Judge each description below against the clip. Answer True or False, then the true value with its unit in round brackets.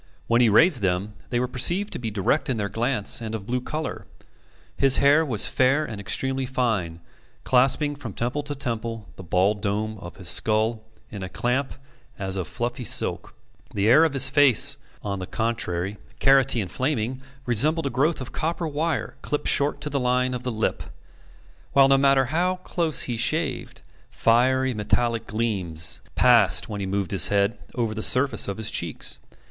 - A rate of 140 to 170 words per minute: False (180 wpm)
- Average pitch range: True (4.6 semitones)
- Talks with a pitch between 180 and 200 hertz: False (120 Hz)